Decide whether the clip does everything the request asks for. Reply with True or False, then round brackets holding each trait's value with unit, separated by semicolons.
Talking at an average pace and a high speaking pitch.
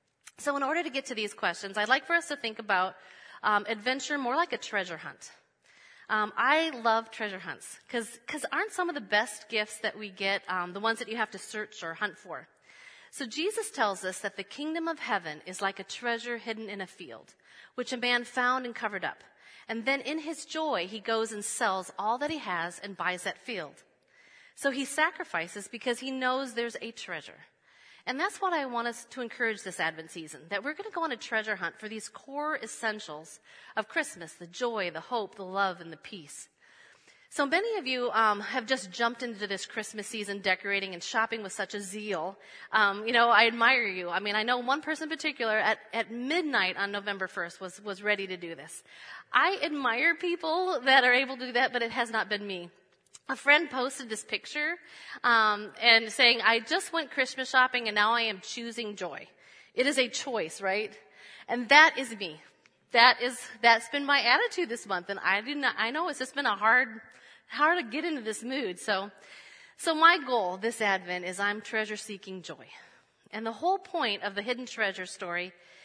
False (210 wpm; 225 Hz)